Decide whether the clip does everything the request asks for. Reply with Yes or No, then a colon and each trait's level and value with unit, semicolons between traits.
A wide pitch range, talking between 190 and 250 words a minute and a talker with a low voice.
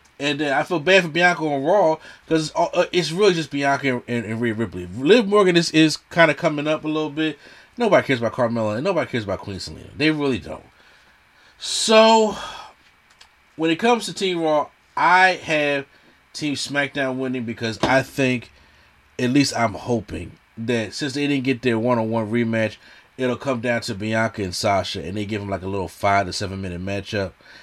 Yes: wide, 6.1 semitones; average, 200 wpm; low, 130 Hz